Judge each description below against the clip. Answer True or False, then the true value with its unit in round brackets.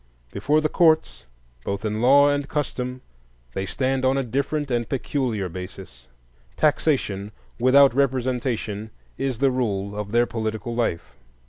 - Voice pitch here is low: True (125 Hz)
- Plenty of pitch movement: False (4.6 semitones)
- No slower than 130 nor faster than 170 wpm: True (135 wpm)